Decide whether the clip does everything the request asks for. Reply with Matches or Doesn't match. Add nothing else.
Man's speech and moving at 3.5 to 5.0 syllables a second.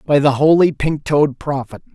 Matches